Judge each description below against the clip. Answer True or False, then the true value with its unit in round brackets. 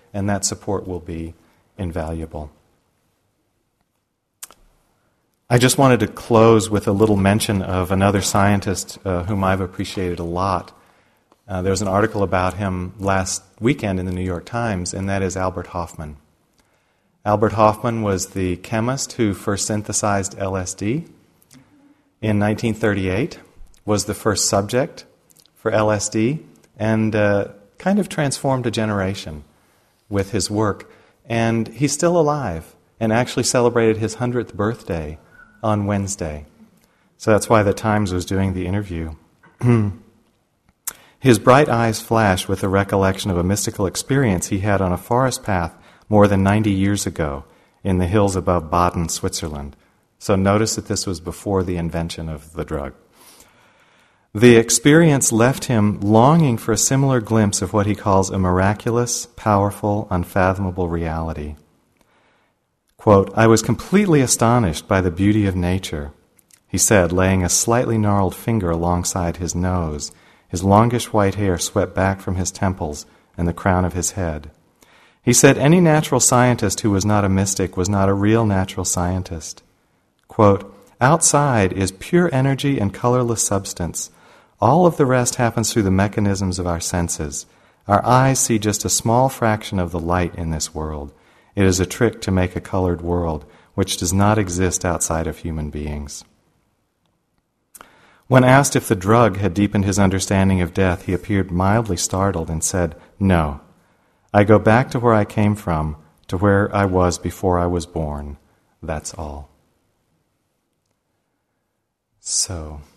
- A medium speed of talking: True (150 wpm)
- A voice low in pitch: True (100 Hz)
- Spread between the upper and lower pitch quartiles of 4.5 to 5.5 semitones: False (3.7 semitones)